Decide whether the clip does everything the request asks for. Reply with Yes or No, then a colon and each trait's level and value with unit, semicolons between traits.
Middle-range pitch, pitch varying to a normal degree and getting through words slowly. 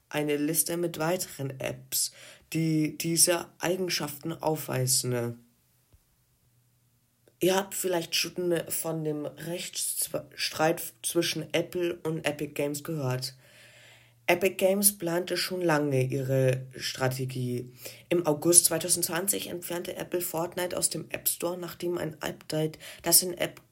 Yes: medium, 160 Hz; average, 4.7 semitones; slow, 115 wpm